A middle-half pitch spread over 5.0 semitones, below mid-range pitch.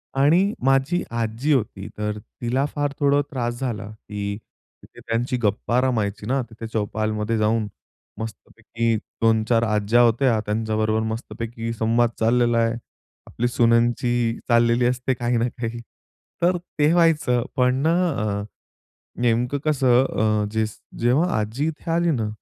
No: average, 2.9 semitones; low, 120 Hz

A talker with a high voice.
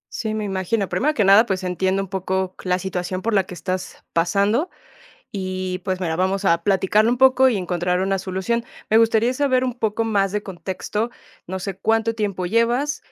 Yes: high, 195 Hz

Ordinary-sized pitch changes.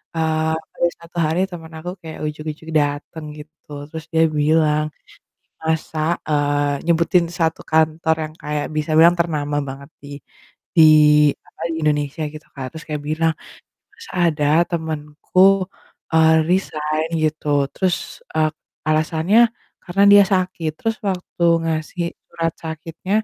No: narrow, 1.9 semitones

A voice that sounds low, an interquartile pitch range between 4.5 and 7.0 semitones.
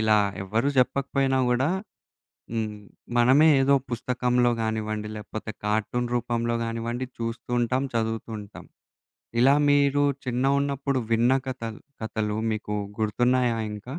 No: low, 120 Hz; average, 2.8 semitones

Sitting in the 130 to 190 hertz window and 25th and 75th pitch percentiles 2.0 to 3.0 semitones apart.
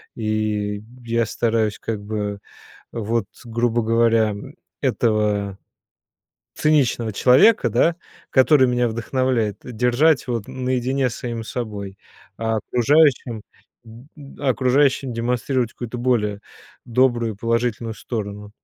No: low, 115 Hz; average, 2.7 semitones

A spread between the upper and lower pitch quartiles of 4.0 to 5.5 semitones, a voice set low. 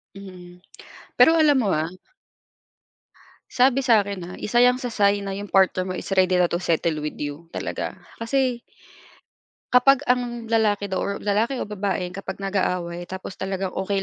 No: average, 4.6 semitones; high, 200 Hz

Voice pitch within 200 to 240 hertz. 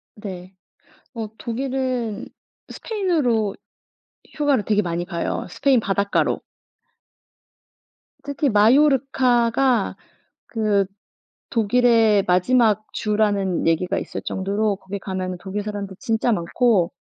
Yes: high, 215 Hz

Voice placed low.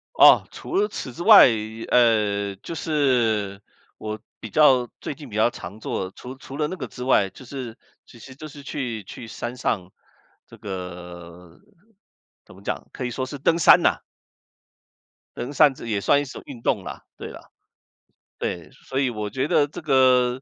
Yes: low, 125 Hz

